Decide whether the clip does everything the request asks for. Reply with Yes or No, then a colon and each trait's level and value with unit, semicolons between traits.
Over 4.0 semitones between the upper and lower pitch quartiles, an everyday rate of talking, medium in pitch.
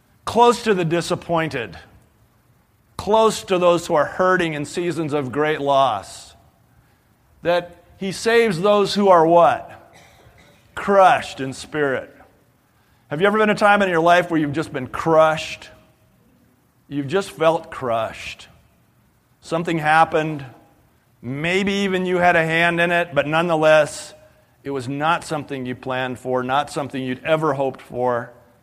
Yes: average, 4.4 semitones; average, 145 wpm; medium, 160 Hz